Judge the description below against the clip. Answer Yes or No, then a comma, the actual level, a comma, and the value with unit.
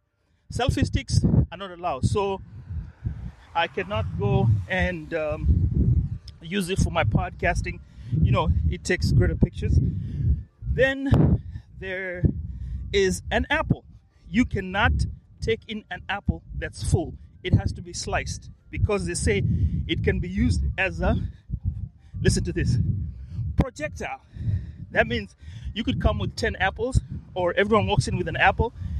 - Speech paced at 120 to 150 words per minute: Yes, fast, 140 wpm